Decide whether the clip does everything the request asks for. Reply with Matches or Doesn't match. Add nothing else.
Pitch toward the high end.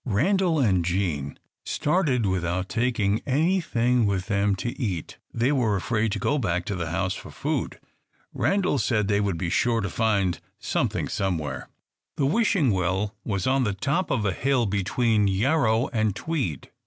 Doesn't match